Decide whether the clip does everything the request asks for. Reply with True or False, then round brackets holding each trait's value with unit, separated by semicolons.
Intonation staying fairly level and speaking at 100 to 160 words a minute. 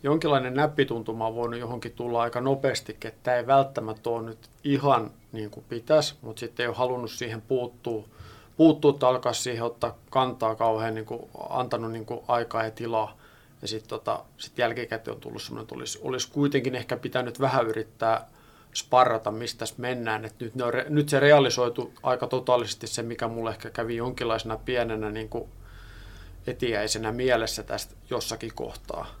False (2.2 semitones; 170 wpm)